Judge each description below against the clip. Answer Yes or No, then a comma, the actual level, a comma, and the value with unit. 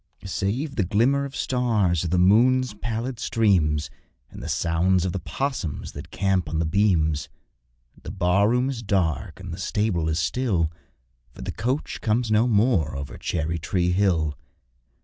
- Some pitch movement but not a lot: No, wide, 5.9 semitones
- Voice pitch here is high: No, very low, 95 Hz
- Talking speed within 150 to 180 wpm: Yes, average, 165 wpm